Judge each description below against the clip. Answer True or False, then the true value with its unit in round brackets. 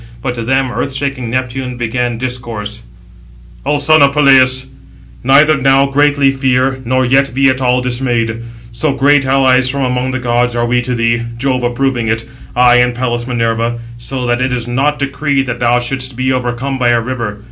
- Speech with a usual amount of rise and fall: False (1.9 semitones)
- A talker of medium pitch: False (125 Hz)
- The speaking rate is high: False (185 wpm)